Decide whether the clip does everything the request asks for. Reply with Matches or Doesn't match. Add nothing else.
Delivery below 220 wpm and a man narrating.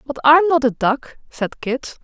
Doesn't match